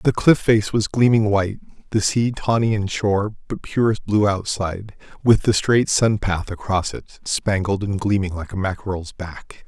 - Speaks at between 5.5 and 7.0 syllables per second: No, 4.5 syllables/s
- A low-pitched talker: Yes, low, 100 Hz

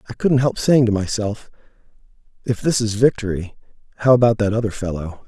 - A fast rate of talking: No, average, 170 wpm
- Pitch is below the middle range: Yes, low, 110 Hz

